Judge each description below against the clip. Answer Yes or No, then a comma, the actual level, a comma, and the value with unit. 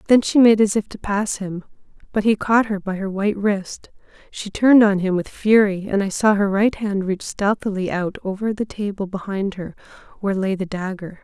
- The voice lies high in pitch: Yes, high, 200 Hz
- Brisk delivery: Yes, fast, 215 wpm